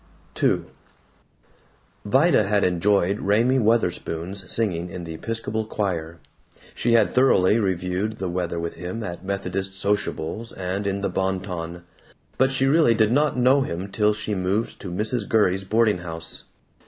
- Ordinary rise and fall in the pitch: Yes, average, 3.8 semitones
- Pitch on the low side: Yes, low, 100 Hz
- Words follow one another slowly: No, average, 150 wpm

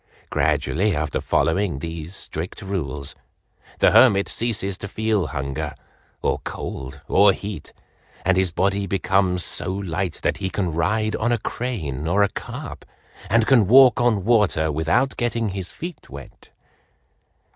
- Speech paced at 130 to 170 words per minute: Yes, average, 145 wpm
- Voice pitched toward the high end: No, very low, 95 Hz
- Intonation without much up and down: No, average, 5.2 semitones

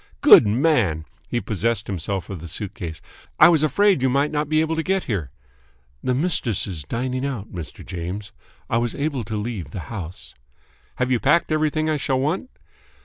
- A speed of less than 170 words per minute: No, average, 185 wpm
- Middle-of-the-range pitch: No, low, 120 Hz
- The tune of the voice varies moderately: No, wide, 7.5 semitones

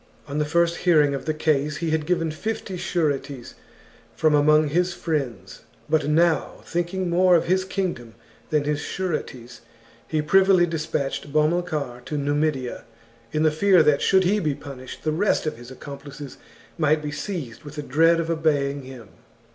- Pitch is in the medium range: Yes, medium, 155 Hz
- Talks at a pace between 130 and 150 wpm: No, average, 165 wpm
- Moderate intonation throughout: Yes, average, 3.2 semitones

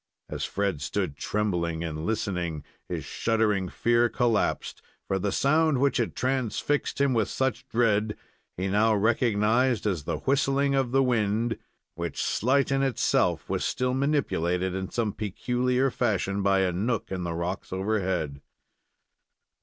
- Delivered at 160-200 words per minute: No, average, 145 wpm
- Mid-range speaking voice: No, low, 110 Hz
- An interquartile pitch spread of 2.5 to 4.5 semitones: No, average, 5.1 semitones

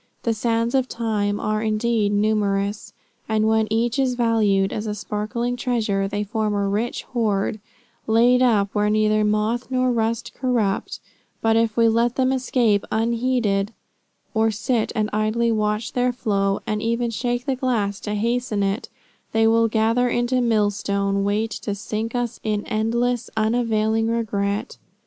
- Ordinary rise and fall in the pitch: No, narrow, 2.2 semitones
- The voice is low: No, high, 220 Hz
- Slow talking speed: No, average, 155 wpm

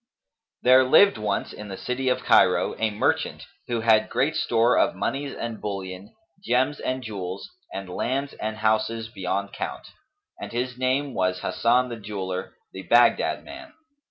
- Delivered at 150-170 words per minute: Yes, average, 155 wpm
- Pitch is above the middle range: No, low, 115 Hz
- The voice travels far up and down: No, average, 4.3 semitones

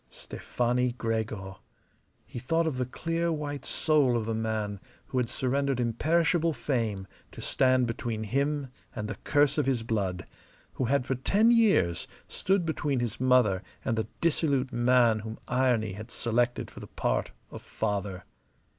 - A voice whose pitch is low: Yes, low, 125 Hz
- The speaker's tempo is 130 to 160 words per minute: Yes, average, 155 wpm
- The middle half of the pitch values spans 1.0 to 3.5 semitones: No, average, 4.2 semitones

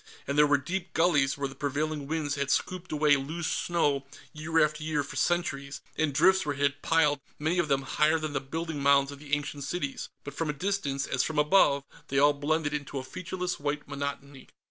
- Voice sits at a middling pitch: Yes, medium, 145 Hz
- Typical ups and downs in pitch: No, narrow, 2.3 semitones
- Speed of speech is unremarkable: No, fast, 210 wpm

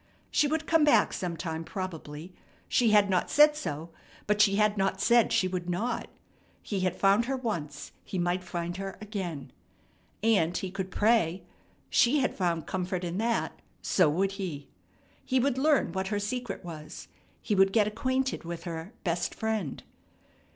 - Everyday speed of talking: Yes, average, 165 wpm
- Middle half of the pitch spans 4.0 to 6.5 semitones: Yes, average, 4.4 semitones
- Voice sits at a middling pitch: No, high, 195 Hz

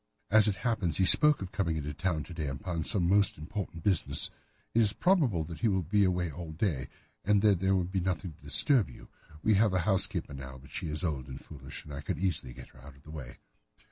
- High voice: No, very low, 90 Hz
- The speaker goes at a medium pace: No, fast, 240 wpm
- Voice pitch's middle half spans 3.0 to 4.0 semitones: No, average, 4.9 semitones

